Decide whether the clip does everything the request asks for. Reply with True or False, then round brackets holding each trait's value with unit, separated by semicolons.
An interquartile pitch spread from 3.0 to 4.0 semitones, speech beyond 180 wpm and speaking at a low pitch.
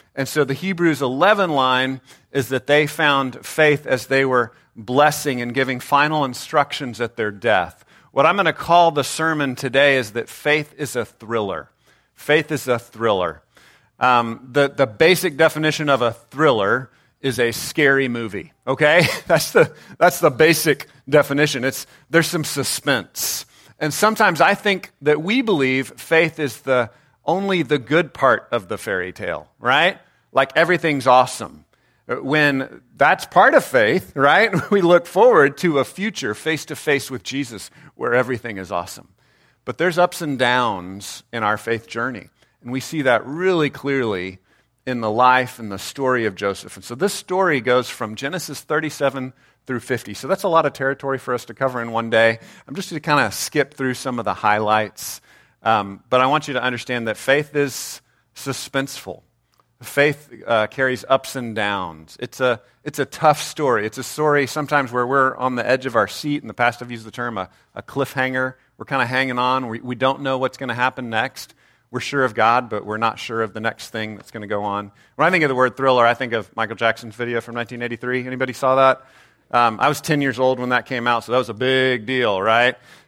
True (3.6 semitones; 200 wpm; 130 Hz)